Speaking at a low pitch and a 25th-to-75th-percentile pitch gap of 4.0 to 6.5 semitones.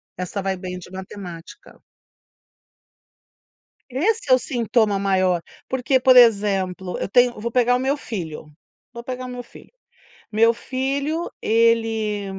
No: high, 230 Hz; average, 4.7 semitones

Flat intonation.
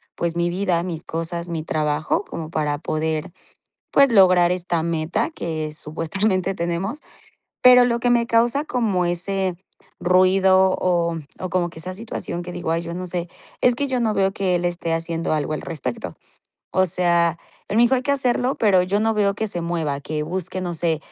No: average, 3.2 semitones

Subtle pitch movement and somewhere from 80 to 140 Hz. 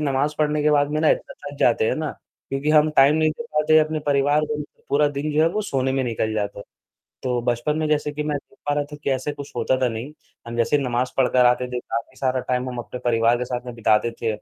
No: average, 3.5 semitones; low, 135 Hz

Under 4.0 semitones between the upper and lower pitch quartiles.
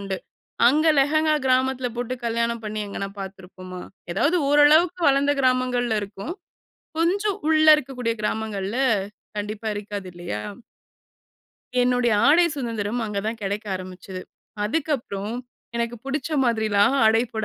No: average, 5.0 semitones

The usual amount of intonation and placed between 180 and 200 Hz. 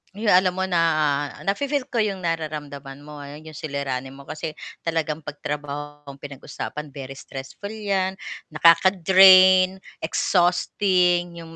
No: average, 4.4 semitones; medium, 165 Hz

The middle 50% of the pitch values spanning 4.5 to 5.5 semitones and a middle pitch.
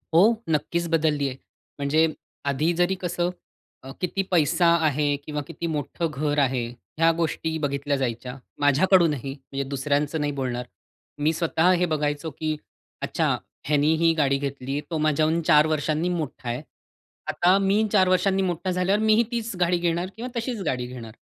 No: average, 3.7 semitones; medium, 155 Hz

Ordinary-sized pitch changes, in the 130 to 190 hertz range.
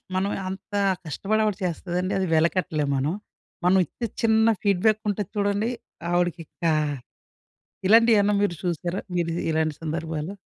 Yes: average, 3.6 semitones; medium, 185 Hz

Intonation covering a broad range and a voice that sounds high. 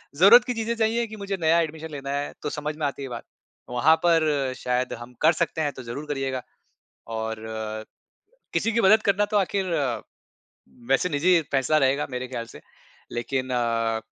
No: wide, 5.9 semitones; medium, 150 Hz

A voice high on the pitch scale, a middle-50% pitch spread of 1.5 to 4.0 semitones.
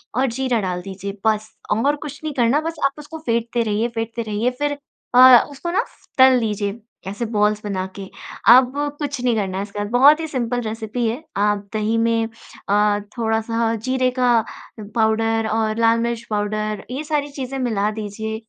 Yes: high, 225 Hz; average, 3.2 semitones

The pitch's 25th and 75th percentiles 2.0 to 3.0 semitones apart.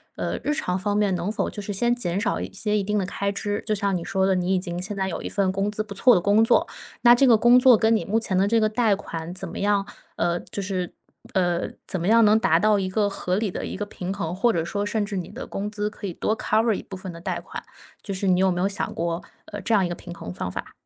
Yes: narrow, 2.6 semitones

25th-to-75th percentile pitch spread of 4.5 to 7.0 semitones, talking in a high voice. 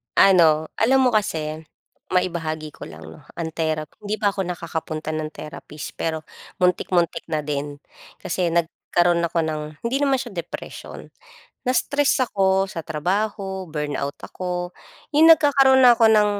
No: average, 5.1 semitones; medium, 175 Hz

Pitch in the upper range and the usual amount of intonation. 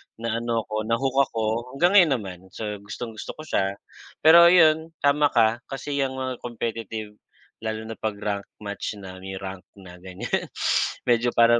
No: low, 115 Hz; average, 4.7 semitones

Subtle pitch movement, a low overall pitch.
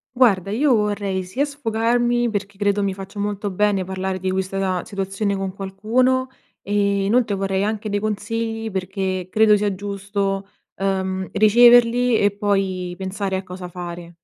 No: narrow, 2.2 semitones; high, 200 Hz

